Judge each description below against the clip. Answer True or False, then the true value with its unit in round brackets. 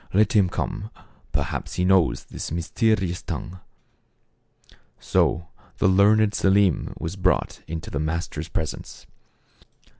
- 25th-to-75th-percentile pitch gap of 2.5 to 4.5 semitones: True (3.4 semitones)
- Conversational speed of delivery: False (115 wpm)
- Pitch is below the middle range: True (95 Hz)